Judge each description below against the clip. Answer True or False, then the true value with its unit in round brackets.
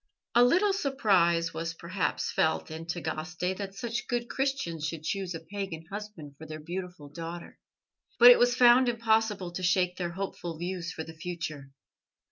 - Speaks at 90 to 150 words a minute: False (165 wpm)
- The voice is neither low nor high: True (180 Hz)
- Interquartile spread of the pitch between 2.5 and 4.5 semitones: False (5.1 semitones)